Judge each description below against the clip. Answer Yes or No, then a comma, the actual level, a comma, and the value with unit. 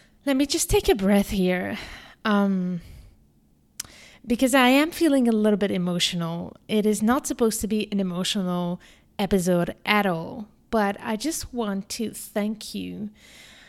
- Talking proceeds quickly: No, average, 150 wpm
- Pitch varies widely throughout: No, average, 4.2 semitones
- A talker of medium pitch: No, high, 210 Hz